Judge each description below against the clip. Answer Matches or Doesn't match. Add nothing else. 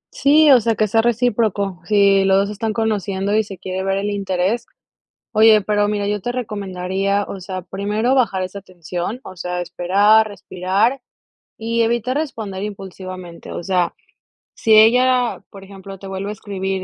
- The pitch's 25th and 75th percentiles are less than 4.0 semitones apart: Matches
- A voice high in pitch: Matches